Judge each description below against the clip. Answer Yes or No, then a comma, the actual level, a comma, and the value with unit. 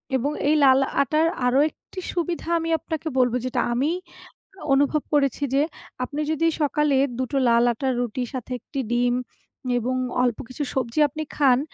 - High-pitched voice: Yes, very high, 275 Hz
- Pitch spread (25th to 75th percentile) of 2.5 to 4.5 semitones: Yes, average, 3.4 semitones